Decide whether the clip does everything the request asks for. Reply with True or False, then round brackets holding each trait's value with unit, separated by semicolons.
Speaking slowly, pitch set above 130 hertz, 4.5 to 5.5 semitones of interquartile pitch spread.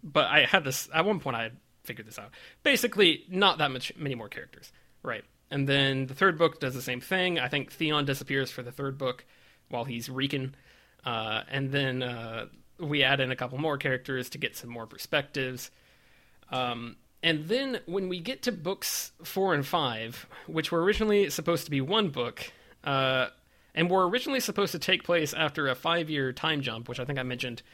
False (205 wpm; 140 Hz; 5.1 semitones)